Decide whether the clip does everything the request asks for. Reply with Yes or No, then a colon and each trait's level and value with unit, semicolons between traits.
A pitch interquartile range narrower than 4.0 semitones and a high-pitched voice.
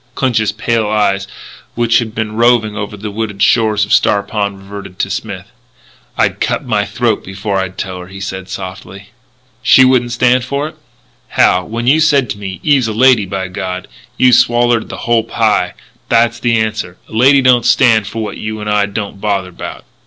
No: average, 3.2 semitones; low, 110 Hz